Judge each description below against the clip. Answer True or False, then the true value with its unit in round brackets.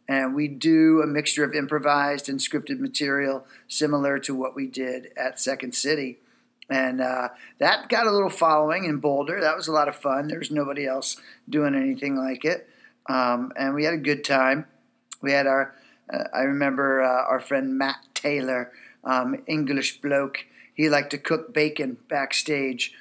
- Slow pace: False (175 wpm)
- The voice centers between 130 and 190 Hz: True (140 Hz)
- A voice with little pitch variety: True (2.2 semitones)